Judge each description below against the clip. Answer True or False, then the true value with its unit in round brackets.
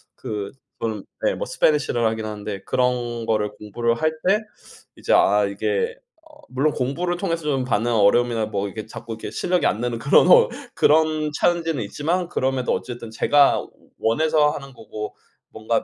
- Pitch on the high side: False (120 Hz)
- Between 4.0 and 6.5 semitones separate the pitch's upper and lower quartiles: True (5.8 semitones)